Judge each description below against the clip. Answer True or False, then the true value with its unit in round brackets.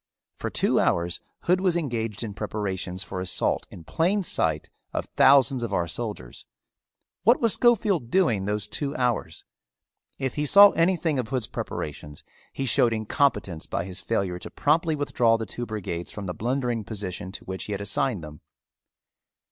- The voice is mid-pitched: False (115 Hz)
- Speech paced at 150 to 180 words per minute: True (165 wpm)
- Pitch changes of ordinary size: False (7.2 semitones)